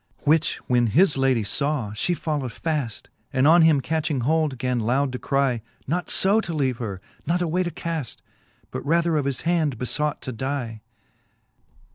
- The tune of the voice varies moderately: Yes, average, 4.4 semitones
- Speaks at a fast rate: No, average, 175 wpm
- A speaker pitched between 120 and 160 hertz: Yes, medium, 140 Hz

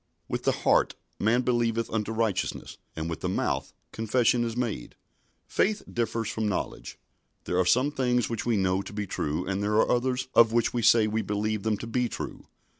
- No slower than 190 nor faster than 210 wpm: Yes, average, 195 wpm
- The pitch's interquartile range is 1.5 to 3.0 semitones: Yes, narrow, 2.5 semitones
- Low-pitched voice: Yes, low, 115 Hz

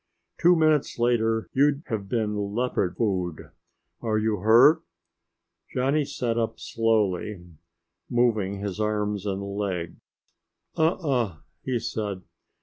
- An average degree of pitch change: Yes, average, 3.5 semitones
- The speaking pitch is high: No, low, 110 Hz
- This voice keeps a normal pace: No, slow, 115 wpm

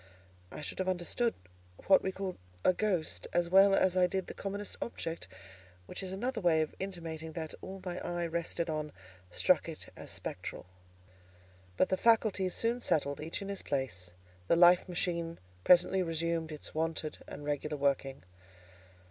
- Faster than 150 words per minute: Yes, average, 165 wpm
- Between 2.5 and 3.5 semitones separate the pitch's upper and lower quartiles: Yes, average, 3.2 semitones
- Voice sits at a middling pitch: Yes, medium, 175 Hz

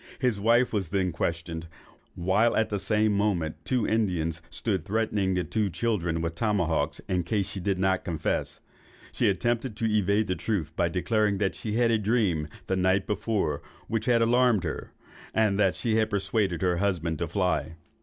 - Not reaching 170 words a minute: No, average, 175 wpm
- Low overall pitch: Yes, low, 100 Hz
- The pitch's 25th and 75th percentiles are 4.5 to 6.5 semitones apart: No, average, 4.0 semitones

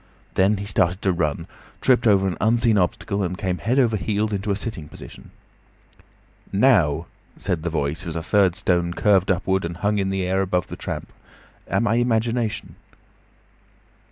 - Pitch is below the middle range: Yes, very low, 95 Hz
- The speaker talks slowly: No, average, 170 wpm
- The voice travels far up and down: No, average, 3.2 semitones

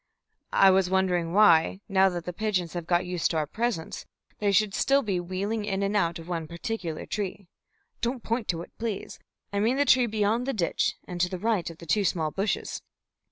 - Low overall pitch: No, high, 190 Hz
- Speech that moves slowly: No, fast, 205 wpm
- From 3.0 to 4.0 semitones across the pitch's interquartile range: Yes, average, 3.6 semitones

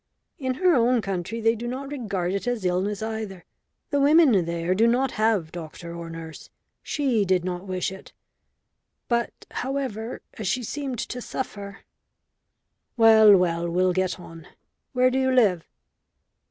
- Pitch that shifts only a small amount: No, wide, 5.5 semitones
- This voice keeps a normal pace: Yes, average, 155 wpm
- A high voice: Yes, high, 215 Hz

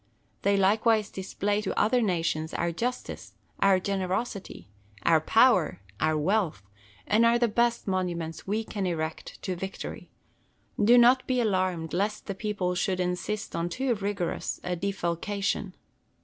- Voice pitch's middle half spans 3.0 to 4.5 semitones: Yes, average, 3.5 semitones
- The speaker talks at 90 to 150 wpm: Yes, average, 140 wpm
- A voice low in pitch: No, high, 195 Hz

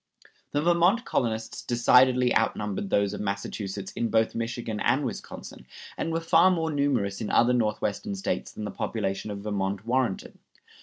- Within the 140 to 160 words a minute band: Yes, average, 155 wpm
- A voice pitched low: Yes, low, 115 Hz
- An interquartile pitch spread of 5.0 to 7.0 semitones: Yes, average, 5.3 semitones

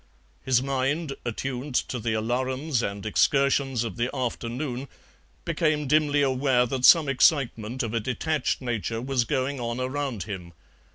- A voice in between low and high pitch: No, low, 130 Hz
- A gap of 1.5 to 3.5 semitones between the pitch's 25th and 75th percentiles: Yes, average, 2.9 semitones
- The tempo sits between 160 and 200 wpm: No, average, 145 wpm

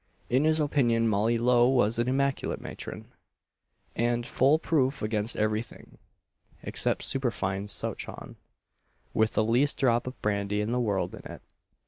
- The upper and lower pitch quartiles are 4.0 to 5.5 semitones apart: No, average, 3.4 semitones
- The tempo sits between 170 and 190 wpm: No, average, 145 wpm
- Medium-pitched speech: No, low, 120 Hz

